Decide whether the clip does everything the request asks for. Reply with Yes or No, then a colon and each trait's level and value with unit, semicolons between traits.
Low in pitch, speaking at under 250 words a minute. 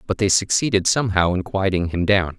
Yes: very low, 95 Hz; average, 200 wpm